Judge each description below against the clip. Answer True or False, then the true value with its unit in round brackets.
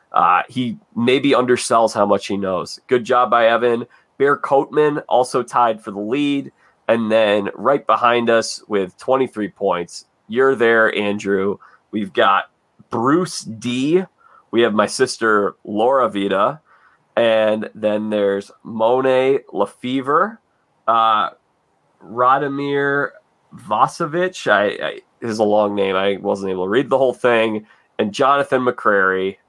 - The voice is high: False (120 Hz)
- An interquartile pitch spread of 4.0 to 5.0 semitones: True (4.4 semitones)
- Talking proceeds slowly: True (130 wpm)